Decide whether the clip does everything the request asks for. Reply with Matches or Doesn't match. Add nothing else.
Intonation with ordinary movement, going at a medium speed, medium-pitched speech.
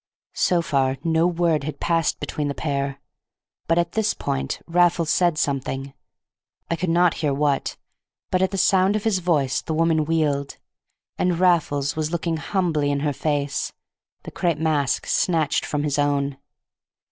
Matches